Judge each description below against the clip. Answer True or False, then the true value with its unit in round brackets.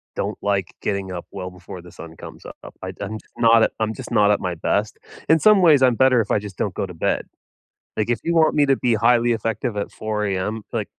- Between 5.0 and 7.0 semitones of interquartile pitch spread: False (3.7 semitones)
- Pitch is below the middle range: True (110 Hz)